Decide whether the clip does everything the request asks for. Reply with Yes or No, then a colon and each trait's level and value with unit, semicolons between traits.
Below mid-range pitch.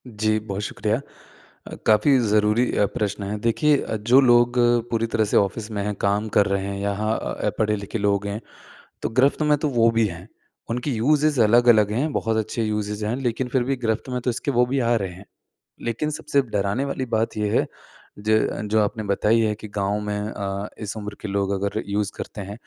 Yes: low, 110 Hz